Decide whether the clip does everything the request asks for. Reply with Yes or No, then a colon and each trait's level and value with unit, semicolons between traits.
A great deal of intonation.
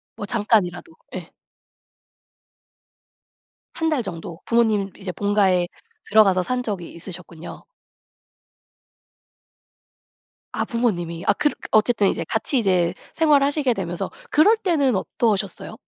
Yes: wide, 5.7 semitones